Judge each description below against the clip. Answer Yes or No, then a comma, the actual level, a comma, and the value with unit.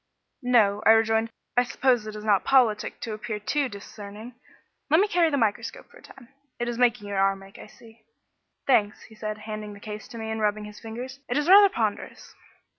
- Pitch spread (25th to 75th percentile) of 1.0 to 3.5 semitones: Yes, average, 2.8 semitones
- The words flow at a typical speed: No, fast, 210 wpm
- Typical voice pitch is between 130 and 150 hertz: No, high, 220 Hz